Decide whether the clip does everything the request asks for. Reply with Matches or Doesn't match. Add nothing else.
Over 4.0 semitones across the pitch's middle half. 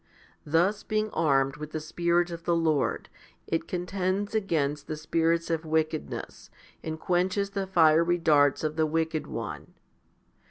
Doesn't match